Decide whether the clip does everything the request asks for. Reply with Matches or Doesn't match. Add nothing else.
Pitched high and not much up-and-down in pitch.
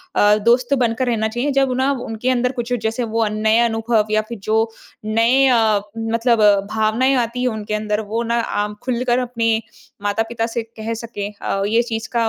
Matches